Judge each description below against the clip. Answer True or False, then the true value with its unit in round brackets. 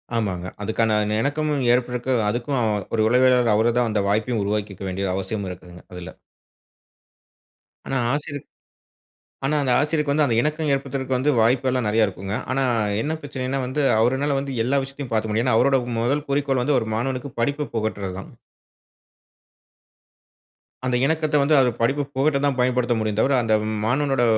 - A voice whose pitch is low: True (125 Hz)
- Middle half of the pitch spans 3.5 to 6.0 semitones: True (4.1 semitones)